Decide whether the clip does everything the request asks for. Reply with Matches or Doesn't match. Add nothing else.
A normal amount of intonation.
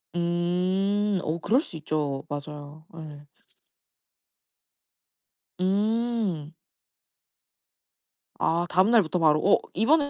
Matches